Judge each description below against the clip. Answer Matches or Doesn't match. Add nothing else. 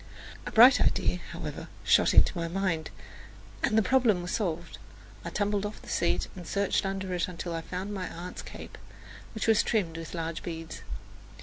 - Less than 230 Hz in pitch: Matches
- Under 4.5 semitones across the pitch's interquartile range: Matches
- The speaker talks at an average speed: Matches